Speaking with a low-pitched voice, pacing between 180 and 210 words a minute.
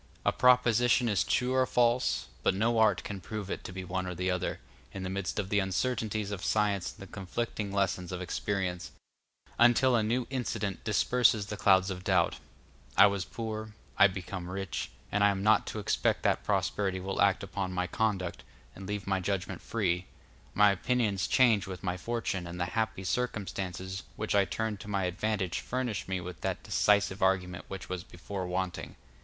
Yes: low, 100 Hz; average, 185 wpm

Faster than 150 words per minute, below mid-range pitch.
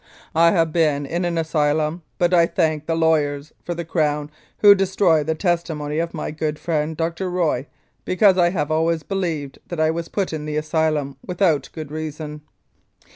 No: average, 175 wpm; medium, 160 Hz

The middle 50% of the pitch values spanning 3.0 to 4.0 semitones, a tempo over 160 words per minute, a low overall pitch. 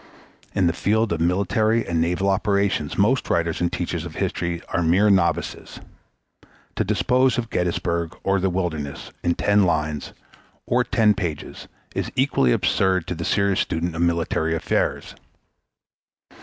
No: average, 3.4 semitones; average, 145 wpm; very low, 90 Hz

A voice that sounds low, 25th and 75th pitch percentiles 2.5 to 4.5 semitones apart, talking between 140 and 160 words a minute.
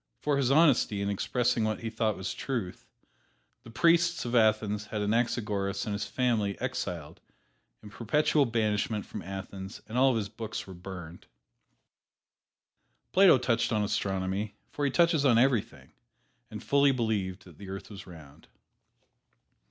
Yes: low, 110 Hz; average, 4.0 semitones; average, 150 wpm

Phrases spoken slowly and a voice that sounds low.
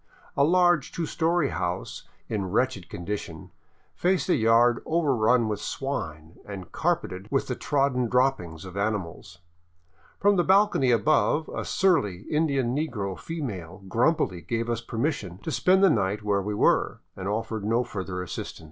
No: average, 155 wpm; low, 115 Hz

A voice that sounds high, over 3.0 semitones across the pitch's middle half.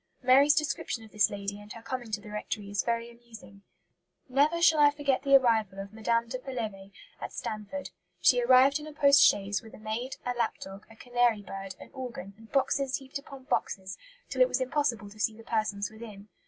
Yes: high, 230 Hz; average, 4.2 semitones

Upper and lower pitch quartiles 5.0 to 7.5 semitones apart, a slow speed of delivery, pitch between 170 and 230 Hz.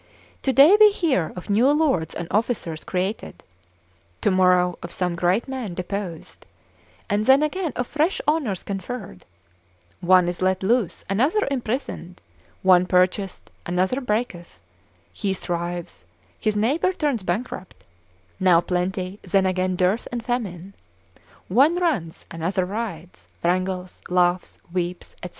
Yes: wide, 5.4 semitones; slow, 125 wpm; high, 190 Hz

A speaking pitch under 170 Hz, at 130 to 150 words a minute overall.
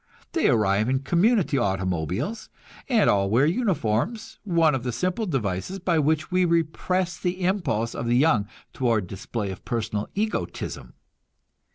Yes: medium, 140 Hz; average, 145 wpm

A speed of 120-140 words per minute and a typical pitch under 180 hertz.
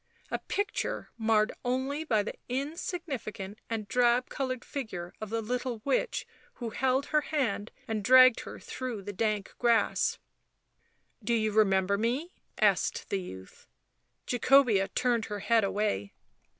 No: slow, 135 wpm; high, 230 Hz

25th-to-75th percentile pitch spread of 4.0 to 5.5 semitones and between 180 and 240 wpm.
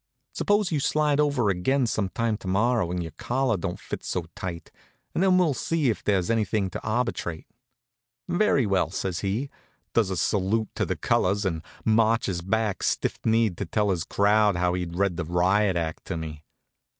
Yes: average, 4.6 semitones; average, 185 wpm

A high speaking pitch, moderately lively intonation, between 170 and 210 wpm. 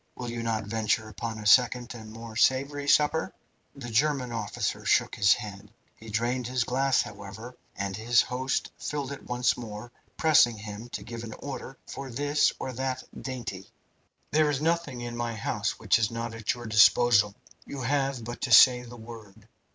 No: low, 120 Hz; average, 3.1 semitones; average, 180 wpm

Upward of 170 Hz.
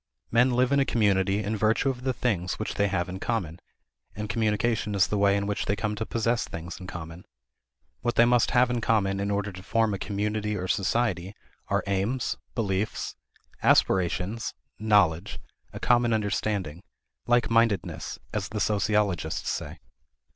No: low, 105 Hz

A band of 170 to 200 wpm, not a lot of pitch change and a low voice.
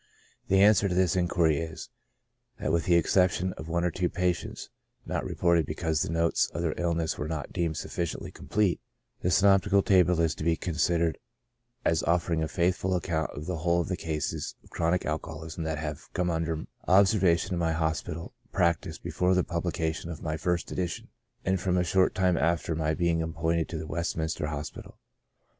Yes: average, 190 wpm; narrow, 2.1 semitones; very low, 85 Hz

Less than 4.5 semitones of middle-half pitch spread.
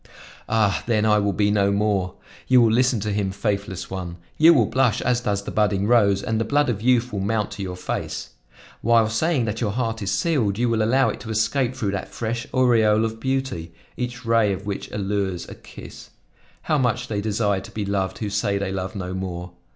Yes: average, 3.2 semitones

